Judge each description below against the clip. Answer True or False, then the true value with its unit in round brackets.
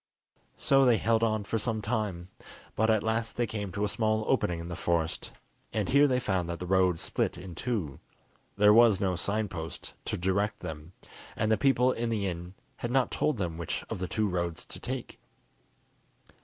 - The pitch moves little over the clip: False (4.3 semitones)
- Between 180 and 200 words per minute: True (195 wpm)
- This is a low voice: True (105 Hz)